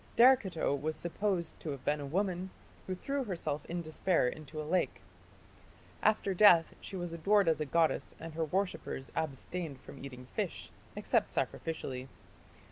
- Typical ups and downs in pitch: Yes, average, 3.7 semitones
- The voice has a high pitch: No, medium, 165 Hz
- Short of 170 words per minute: Yes, average, 160 wpm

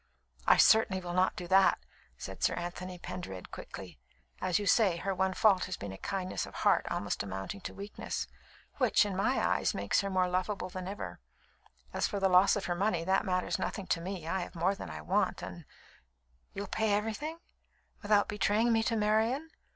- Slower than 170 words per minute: No, average, 195 wpm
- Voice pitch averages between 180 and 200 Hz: Yes, high, 190 Hz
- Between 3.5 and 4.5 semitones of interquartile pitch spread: No, average, 2.7 semitones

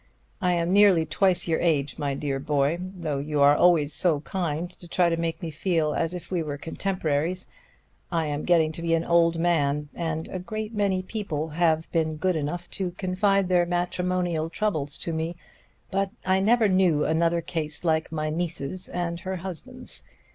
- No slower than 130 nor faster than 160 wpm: No, average, 175 wpm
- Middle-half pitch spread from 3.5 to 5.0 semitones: No, average, 2.7 semitones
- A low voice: No, medium, 170 Hz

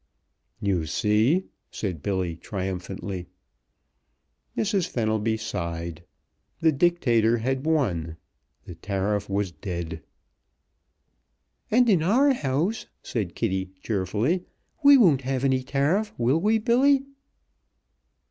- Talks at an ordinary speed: No, slow, 100 wpm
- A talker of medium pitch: No, low, 115 Hz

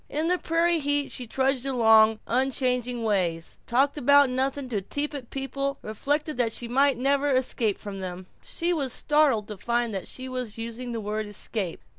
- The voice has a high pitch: Yes, very high, 255 Hz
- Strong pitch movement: No, average, 4.1 semitones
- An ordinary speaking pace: Yes, average, 180 wpm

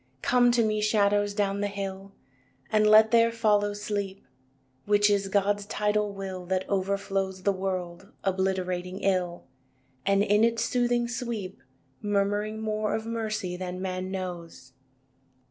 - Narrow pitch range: Yes, narrow, 2.1 semitones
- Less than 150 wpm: Yes, average, 140 wpm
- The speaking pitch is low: No, high, 200 Hz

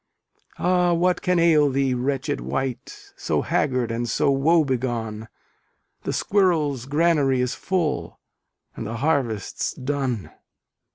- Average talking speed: No, slow, 120 wpm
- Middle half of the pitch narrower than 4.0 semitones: No, average, 4.9 semitones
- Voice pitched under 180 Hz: Yes, medium, 140 Hz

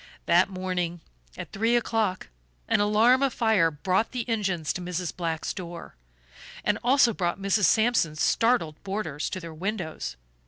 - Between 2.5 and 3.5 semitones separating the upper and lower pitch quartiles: No, average, 4.7 semitones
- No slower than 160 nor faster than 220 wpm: No, average, 150 wpm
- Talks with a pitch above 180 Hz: Yes, high, 190 Hz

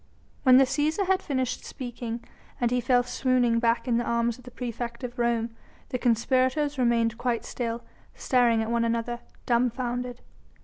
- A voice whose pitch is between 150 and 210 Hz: No, high, 240 Hz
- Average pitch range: No, narrow, 1.5 semitones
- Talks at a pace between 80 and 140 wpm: No, average, 165 wpm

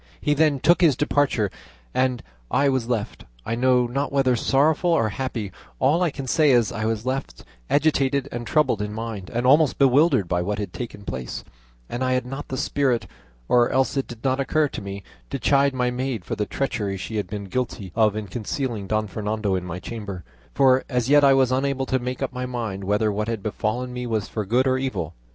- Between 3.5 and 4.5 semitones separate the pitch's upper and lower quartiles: Yes, average, 4.1 semitones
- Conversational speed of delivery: No, fast, 215 wpm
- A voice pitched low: Yes, low, 125 Hz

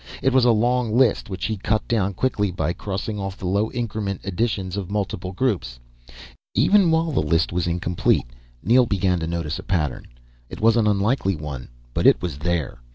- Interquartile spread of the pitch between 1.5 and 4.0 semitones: No, average, 4.7 semitones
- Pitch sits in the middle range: No, low, 100 Hz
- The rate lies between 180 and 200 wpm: Yes, average, 190 wpm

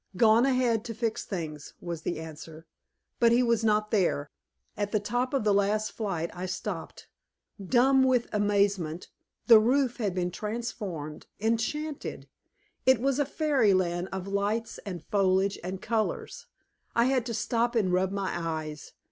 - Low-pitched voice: No, high, 210 Hz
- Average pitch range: Yes, average, 4.4 semitones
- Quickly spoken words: No, average, 155 wpm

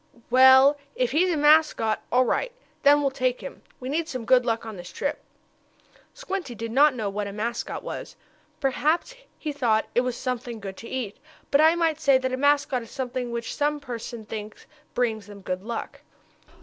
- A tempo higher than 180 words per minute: Yes, average, 190 wpm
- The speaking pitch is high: Yes, very high, 255 Hz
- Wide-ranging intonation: No, average, 4.0 semitones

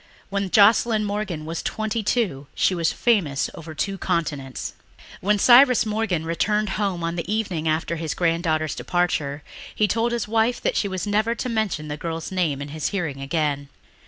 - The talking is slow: No, average, 175 wpm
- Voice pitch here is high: No, medium, 180 Hz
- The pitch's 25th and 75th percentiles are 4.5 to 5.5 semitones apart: Yes, average, 5.2 semitones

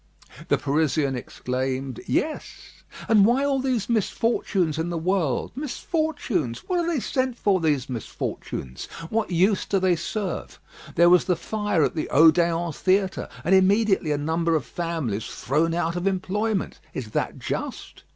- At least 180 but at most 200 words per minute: No, average, 150 wpm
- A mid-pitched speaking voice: Yes, medium, 175 Hz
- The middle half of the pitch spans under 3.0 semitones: No, wide, 5.4 semitones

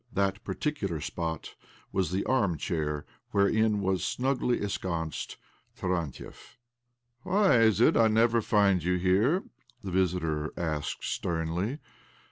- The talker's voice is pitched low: Yes, very low, 95 Hz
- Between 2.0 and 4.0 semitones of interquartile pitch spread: No, average, 5.3 semitones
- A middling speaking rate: No, slow, 125 wpm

